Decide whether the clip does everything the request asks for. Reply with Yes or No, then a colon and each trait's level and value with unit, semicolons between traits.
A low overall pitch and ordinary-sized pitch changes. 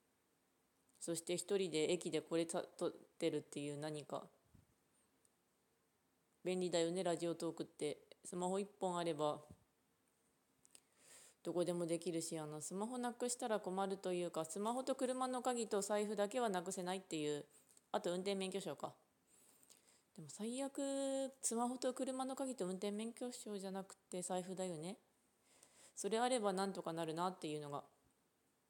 No: medium, 185 Hz; average, 5.0 semitones